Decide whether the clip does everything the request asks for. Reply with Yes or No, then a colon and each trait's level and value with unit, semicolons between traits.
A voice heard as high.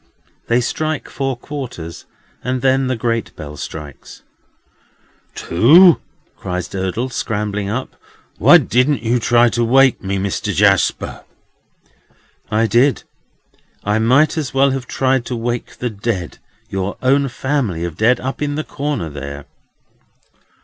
No: low, 120 Hz